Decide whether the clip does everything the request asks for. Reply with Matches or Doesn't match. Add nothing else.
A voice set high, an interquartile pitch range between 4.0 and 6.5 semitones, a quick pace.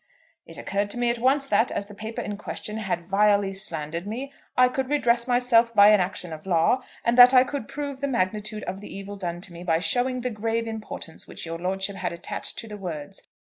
Matches